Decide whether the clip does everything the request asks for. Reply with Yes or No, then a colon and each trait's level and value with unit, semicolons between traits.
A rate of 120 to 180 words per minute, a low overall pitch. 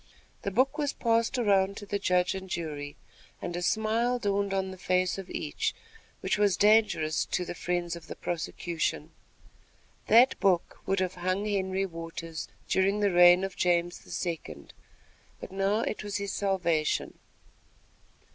No: average, 155 wpm; high, 190 Hz